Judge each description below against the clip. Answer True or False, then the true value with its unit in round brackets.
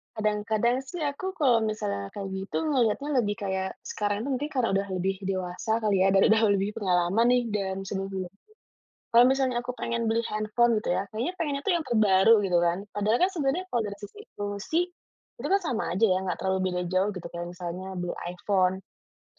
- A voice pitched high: True (210 Hz)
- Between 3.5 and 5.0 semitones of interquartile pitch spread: True (4.0 semitones)